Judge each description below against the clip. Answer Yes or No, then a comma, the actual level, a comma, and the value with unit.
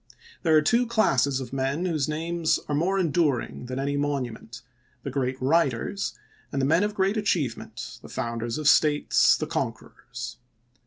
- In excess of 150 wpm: Yes, average, 165 wpm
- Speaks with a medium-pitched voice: Yes, medium, 145 Hz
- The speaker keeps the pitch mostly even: No, average, 4.7 semitones